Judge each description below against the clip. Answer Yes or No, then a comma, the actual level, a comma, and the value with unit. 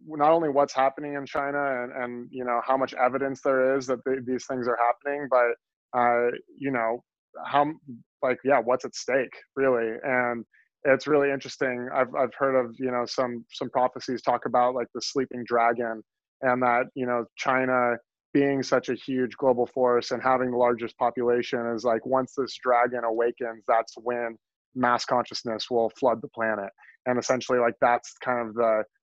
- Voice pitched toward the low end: Yes, low, 125 Hz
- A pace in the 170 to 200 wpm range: Yes, average, 180 wpm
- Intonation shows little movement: Yes, narrow, 1.8 semitones